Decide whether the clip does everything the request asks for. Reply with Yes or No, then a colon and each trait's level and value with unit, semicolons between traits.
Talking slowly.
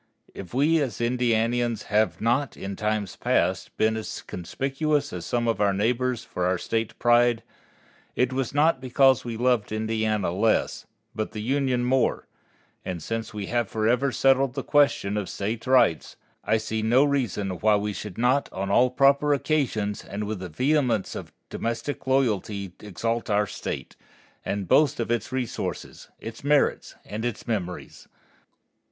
No: average, 160 wpm